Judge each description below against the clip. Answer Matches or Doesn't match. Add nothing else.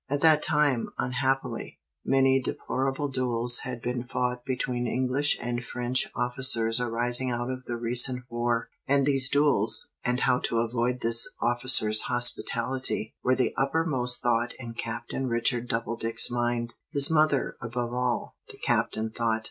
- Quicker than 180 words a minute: Doesn't match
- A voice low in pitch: Matches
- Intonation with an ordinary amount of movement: Doesn't match